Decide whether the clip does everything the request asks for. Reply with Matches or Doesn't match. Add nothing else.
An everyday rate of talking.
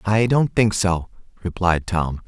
Matches